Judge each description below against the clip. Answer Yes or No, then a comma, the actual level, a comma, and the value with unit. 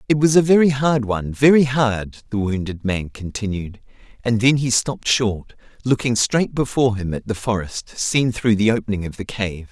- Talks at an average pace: Yes, average, 185 wpm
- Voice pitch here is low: Yes, low, 115 Hz